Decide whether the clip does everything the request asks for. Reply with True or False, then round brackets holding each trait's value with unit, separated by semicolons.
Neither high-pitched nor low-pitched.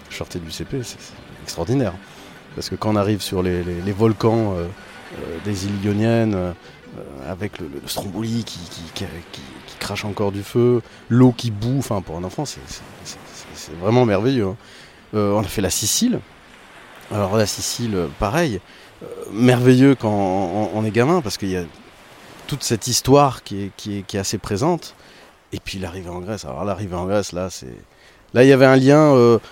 False (105 Hz)